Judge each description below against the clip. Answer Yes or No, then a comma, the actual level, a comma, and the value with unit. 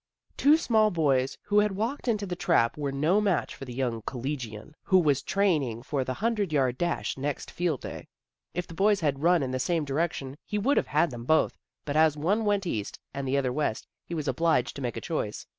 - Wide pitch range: Yes, wide, 6.0 semitones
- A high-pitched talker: No, medium, 155 Hz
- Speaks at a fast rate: Yes, fast, 225 wpm